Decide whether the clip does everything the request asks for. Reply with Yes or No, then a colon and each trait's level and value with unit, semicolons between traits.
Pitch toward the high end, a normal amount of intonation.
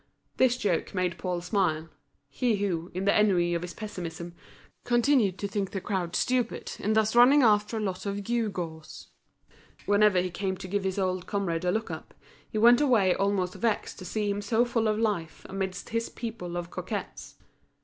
Yes: high, 200 Hz; average, 3.4 semitones